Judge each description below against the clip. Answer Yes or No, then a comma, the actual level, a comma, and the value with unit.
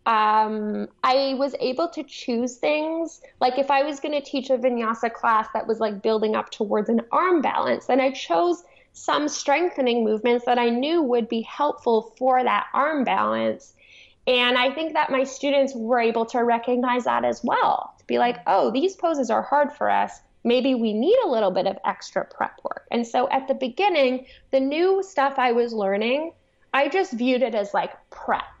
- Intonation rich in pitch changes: No, average, 3.5 semitones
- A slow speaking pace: No, average, 195 wpm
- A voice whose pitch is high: Yes, very high, 255 Hz